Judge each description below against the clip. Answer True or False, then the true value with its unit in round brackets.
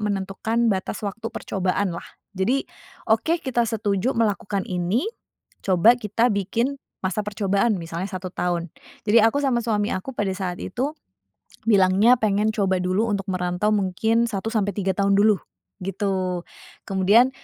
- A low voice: False (200 Hz)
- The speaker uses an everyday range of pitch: True (3.1 semitones)